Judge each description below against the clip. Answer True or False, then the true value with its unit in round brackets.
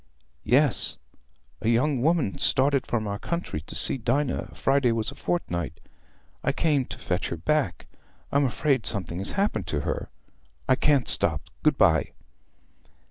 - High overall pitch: False (130 Hz)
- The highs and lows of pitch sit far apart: True (7.2 semitones)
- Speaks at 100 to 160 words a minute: True (150 wpm)